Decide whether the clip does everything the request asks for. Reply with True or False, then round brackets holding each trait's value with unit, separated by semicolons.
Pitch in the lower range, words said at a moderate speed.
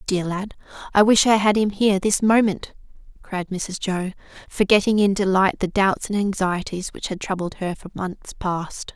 False (195 Hz; 180 wpm)